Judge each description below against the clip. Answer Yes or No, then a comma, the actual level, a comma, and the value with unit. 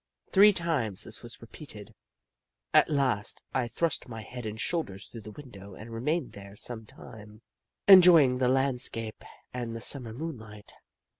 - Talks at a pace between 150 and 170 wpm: Yes, average, 155 wpm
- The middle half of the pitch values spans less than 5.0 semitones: Yes, average, 4.6 semitones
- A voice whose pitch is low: Yes, low, 120 Hz